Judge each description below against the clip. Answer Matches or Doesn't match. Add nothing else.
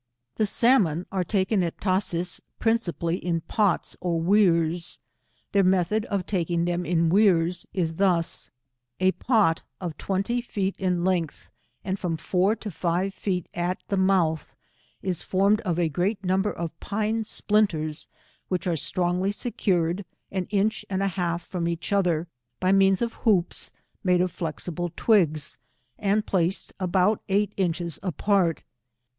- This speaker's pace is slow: Doesn't match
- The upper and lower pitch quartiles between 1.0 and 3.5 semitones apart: Matches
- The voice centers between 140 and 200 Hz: Matches